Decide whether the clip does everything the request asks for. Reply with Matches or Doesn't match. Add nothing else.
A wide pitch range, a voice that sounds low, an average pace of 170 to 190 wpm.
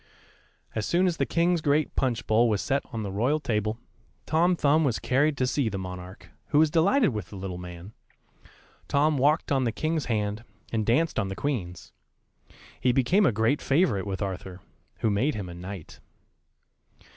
Matches